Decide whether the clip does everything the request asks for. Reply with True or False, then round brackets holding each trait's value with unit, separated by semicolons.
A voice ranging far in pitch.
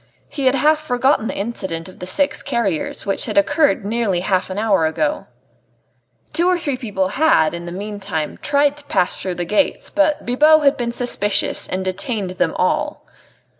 True (7.4 semitones)